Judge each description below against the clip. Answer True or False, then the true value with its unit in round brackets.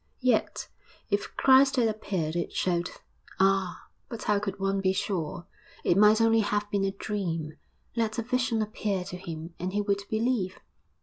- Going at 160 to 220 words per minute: True (170 wpm)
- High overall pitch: True (200 Hz)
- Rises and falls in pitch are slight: False (3.0 semitones)